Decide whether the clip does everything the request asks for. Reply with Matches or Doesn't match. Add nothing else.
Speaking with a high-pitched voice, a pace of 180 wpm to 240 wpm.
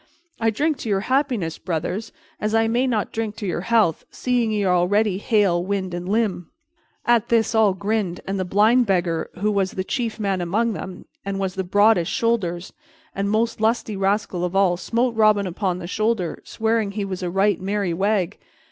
Matches